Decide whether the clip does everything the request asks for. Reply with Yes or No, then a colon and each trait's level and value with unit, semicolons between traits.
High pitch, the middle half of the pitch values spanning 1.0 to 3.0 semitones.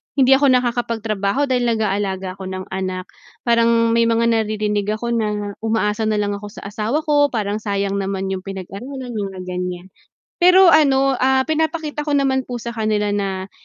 No: high, 220 Hz; average, 4.6 semitones